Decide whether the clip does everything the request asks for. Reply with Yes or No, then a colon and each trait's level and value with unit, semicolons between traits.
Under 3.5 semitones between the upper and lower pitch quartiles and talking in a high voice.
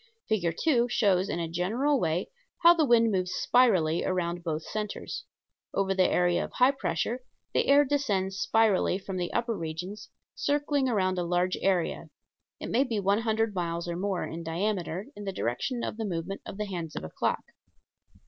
No: average, 4.7 semitones; high, 195 Hz